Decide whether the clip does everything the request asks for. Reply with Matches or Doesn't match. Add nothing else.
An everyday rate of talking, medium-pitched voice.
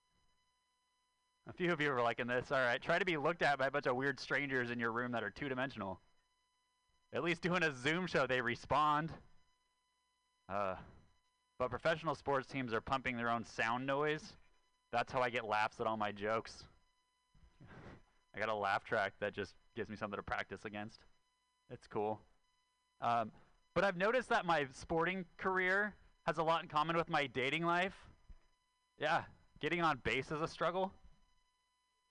Matches